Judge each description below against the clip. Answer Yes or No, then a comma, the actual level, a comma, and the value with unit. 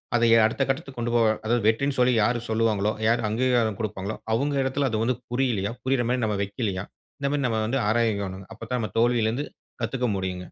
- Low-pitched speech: Yes, low, 115 Hz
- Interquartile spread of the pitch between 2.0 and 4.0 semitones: Yes, average, 2.9 semitones